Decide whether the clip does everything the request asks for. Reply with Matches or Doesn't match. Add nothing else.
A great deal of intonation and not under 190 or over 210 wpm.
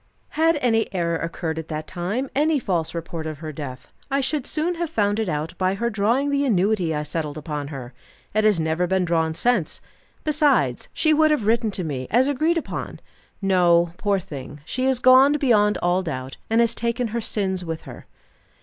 Matches